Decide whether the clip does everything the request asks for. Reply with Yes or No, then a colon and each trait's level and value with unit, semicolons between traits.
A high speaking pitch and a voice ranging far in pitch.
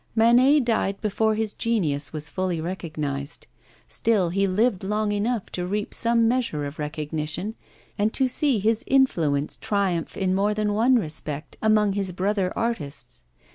Yes: high, 200 Hz; wide, 5.7 semitones